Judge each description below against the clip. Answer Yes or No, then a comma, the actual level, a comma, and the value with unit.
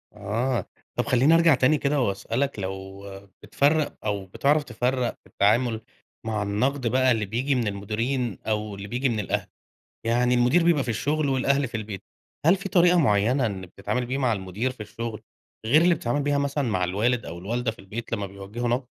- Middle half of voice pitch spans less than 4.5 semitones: No, average, 4.8 semitones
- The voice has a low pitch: Yes, low, 120 Hz